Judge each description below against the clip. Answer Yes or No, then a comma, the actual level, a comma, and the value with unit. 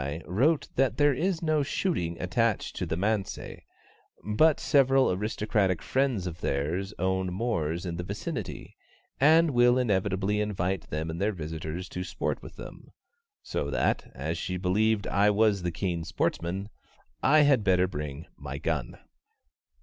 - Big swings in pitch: Yes, wide, 5.8 semitones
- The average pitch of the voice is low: Yes, very low, 95 Hz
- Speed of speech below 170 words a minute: Yes, average, 150 wpm